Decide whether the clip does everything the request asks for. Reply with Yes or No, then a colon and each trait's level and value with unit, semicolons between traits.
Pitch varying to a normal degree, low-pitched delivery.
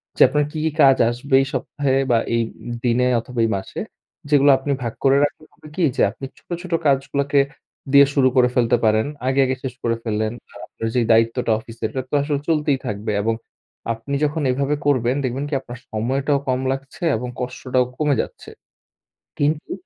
Yes: average, 3.1 semitones; low, 130 Hz